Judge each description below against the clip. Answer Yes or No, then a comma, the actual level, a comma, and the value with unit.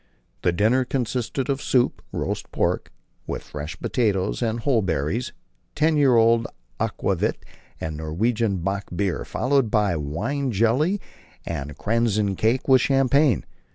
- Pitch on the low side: Yes, low, 115 Hz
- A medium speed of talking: No, slow, 120 wpm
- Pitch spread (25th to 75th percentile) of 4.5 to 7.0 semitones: Yes, wide, 5.4 semitones